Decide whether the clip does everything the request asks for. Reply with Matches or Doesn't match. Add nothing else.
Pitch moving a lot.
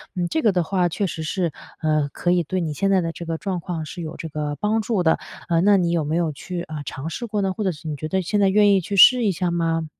Doesn't match